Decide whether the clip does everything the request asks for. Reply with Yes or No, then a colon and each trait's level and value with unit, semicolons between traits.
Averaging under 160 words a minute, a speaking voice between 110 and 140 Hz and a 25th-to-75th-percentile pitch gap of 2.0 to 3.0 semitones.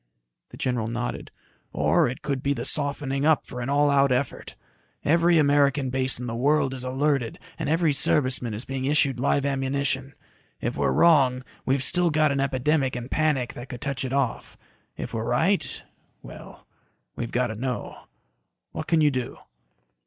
No: average, 175 wpm; low, 135 Hz; narrow, 2.5 semitones